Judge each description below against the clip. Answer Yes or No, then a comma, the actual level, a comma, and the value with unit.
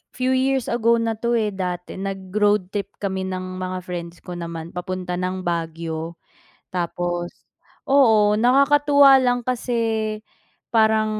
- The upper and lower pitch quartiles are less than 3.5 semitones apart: No, average, 4.6 semitones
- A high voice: Yes, high, 200 Hz